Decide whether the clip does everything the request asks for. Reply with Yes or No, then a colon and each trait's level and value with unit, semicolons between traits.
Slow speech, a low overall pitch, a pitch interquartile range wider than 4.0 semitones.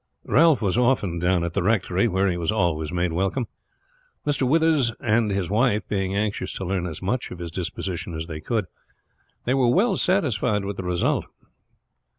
No: average, 180 wpm; low, 100 Hz; wide, 5.4 semitones